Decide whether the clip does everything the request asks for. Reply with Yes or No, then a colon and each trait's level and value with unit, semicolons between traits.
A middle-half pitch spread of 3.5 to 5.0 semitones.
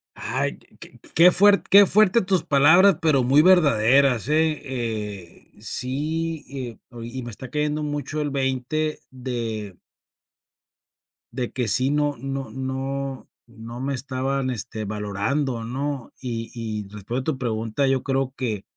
Yes: average, 3.9 semitones